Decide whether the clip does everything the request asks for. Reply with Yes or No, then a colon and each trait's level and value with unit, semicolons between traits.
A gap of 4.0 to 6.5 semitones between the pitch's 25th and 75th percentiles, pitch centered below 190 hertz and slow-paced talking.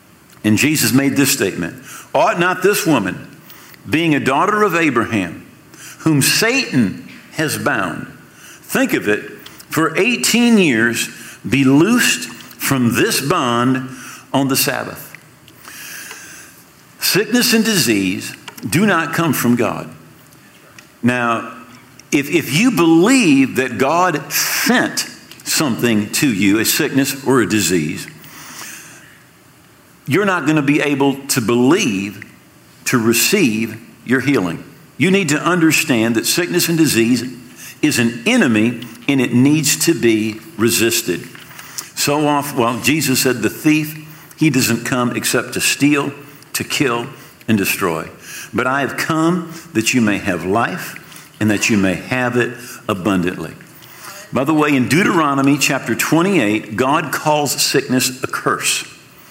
Yes: average, 4.8 semitones; low, 135 Hz; slow, 130 wpm